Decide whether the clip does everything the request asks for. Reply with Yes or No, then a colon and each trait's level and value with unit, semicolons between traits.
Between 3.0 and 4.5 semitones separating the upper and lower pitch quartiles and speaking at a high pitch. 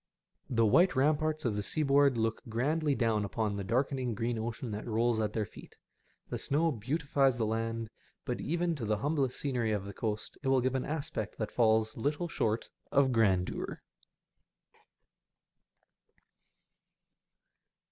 No: average, 4.2 semitones; low, 120 Hz